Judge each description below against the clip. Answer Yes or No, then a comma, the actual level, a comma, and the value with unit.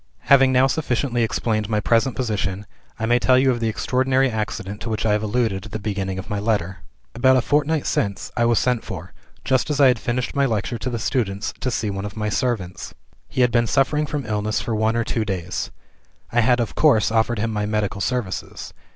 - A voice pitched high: No, low, 115 Hz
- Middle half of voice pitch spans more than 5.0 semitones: No, average, 3.3 semitones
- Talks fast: Yes, fast, 220 wpm